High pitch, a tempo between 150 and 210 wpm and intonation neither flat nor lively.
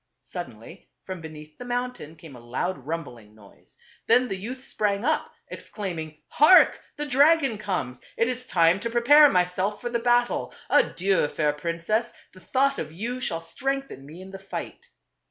No: high, 195 Hz; average, 170 wpm; wide, 7.1 semitones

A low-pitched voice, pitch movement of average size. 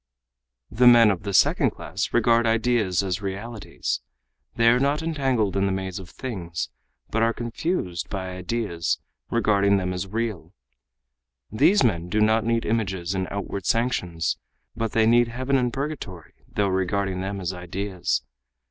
Yes: low, 105 Hz; average, 3.9 semitones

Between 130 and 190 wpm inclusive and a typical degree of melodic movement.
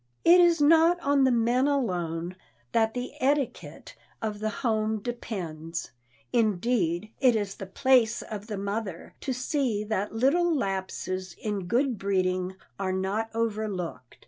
Yes: average, 140 wpm; average, 5.0 semitones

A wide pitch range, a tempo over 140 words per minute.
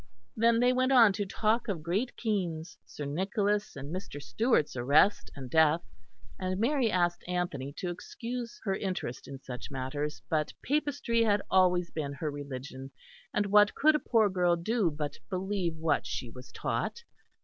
Yes: wide, 6.6 semitones; average, 165 wpm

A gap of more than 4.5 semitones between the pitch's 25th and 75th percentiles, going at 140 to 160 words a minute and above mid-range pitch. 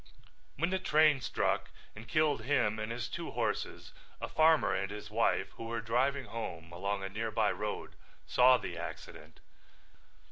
No: average, 5.0 semitones; average, 155 wpm; low, 115 Hz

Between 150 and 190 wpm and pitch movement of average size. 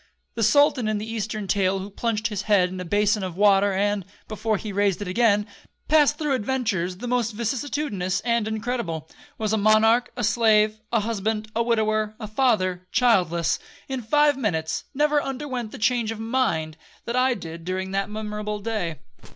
Yes: average, 170 wpm; average, 3.2 semitones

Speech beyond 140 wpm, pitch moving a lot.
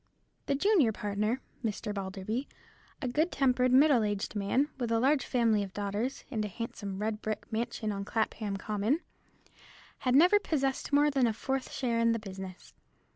No: average, 170 wpm; average, 4.3 semitones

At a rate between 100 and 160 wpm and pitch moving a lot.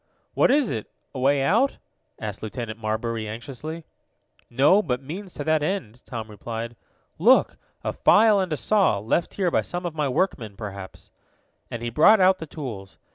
No: average, 175 wpm; wide, 8.0 semitones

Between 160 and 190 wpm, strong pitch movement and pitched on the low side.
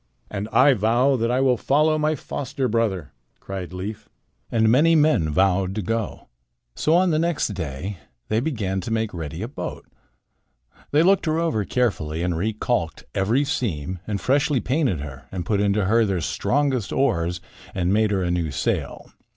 Yes: average, 175 wpm; wide, 6.6 semitones; low, 110 Hz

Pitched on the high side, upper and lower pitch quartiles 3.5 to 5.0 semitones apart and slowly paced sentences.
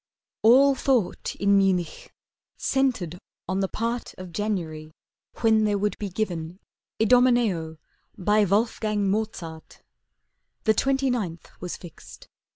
Yes: high, 205 Hz; average, 4.5 semitones; slow, 115 wpm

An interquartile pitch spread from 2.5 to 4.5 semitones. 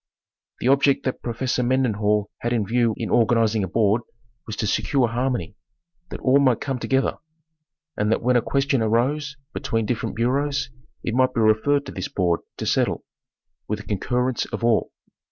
Yes: average, 3.2 semitones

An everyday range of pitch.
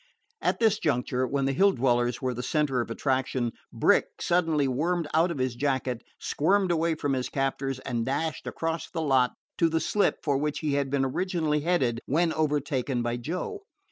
Yes: average, 4.0 semitones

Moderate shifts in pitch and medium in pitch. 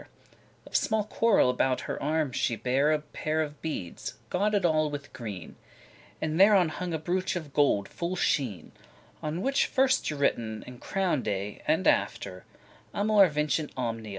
No: wide, 6.3 semitones; medium, 155 Hz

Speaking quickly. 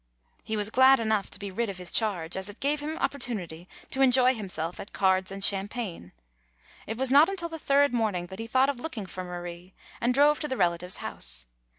Yes: fast, 215 wpm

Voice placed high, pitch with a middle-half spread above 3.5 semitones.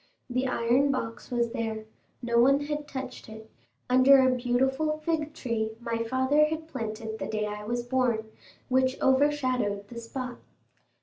No: very high, 250 Hz; average, 2.8 semitones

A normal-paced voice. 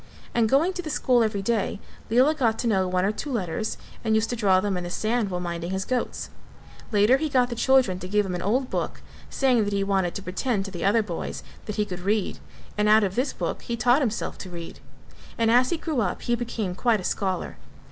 No: fast, 240 wpm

